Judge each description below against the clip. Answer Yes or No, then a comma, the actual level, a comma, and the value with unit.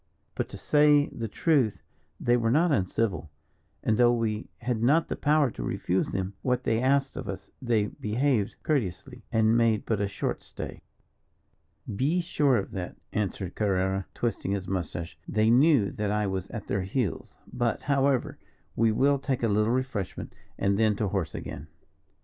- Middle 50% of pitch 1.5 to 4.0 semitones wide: No, average, 4.8 semitones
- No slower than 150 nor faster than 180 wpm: Yes, average, 170 wpm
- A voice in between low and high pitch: No, low, 110 Hz